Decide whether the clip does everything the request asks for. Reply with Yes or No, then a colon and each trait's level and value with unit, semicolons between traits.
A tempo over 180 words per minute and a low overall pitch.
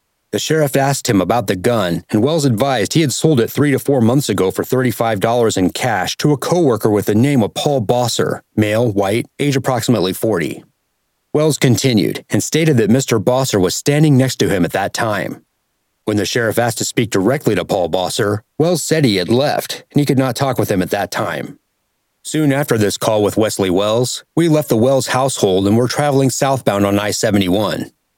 Yes: fast, 205 wpm; low, 125 Hz